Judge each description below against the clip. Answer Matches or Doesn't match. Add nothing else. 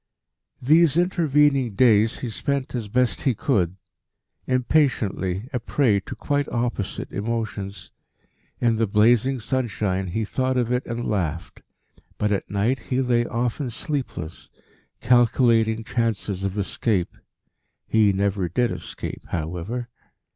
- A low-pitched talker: Matches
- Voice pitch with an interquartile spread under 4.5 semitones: Matches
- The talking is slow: Matches